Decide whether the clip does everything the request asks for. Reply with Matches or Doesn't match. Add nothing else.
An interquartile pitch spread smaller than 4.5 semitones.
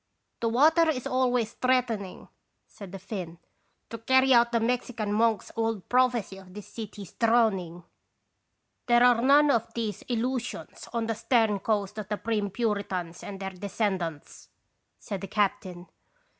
Matches